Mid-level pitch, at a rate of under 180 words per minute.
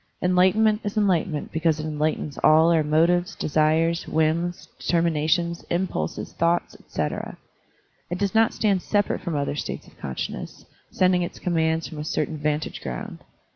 Yes: medium, 165 Hz; average, 150 wpm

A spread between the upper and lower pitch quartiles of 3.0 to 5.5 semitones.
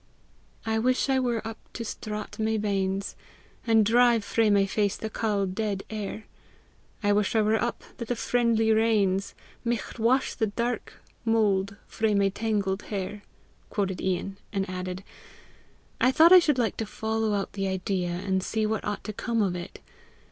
No: narrow, 2.4 semitones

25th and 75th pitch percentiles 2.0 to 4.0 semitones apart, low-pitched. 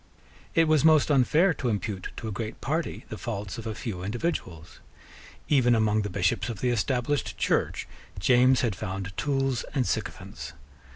No: average, 4.9 semitones; low, 120 Hz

